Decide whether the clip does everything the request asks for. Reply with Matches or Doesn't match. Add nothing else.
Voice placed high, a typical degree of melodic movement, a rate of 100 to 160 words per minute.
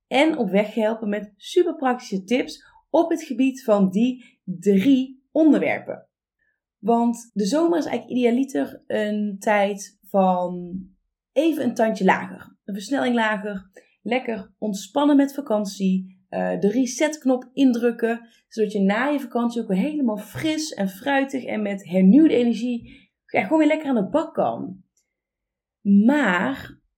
Matches